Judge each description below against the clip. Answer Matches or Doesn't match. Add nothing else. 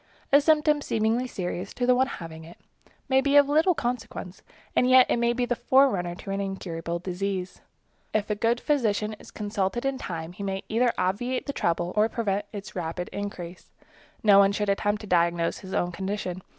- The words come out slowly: Doesn't match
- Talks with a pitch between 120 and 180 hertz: Doesn't match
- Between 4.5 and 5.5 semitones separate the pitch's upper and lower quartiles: Matches